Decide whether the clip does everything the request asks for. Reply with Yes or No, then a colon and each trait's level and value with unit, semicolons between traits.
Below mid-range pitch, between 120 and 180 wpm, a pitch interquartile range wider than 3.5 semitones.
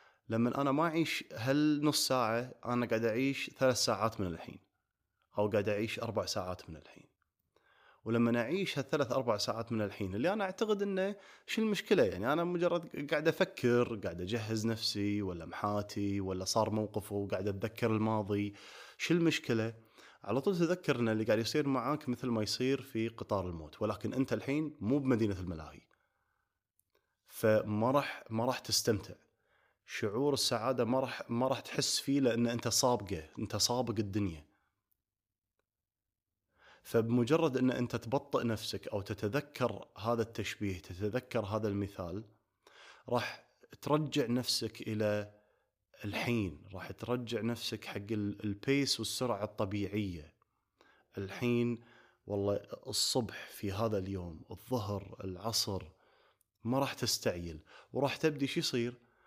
Yes: low, 115 Hz; average, 130 wpm; average, 3.9 semitones